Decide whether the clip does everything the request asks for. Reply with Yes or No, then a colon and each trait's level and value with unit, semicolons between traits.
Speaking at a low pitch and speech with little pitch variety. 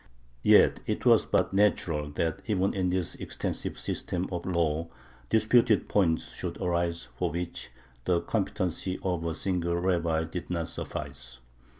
Yes: very low, 85 Hz; narrow, 2.2 semitones